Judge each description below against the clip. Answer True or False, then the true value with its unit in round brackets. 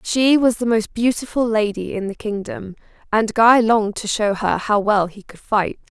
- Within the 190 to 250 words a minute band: True (200 wpm)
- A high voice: True (215 Hz)